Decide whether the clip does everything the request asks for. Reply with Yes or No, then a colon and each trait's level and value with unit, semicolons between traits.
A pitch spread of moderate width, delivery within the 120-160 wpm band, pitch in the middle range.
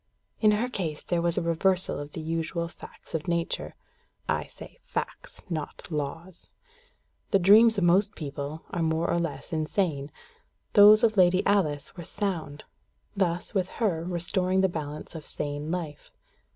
Yes: average, 3.3 semitones; average, 155 wpm; medium, 170 Hz